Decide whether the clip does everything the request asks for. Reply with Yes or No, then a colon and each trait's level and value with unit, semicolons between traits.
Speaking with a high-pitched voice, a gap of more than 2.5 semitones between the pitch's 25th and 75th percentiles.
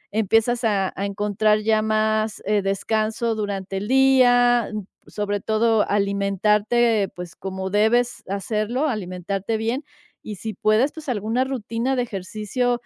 Yes: high, 215 Hz; average, 2.9 semitones